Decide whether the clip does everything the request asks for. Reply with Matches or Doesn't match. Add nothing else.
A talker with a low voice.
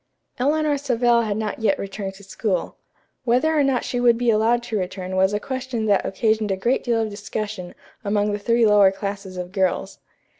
Doesn't match